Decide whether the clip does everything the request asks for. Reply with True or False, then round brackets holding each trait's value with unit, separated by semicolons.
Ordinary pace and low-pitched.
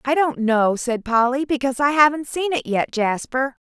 False (195 wpm; 265 Hz)